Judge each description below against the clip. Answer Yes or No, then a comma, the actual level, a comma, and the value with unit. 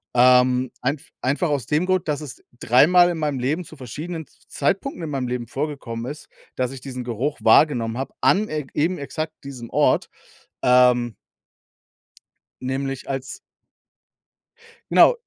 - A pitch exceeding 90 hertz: Yes, low, 135 Hz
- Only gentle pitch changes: No, average, 3.5 semitones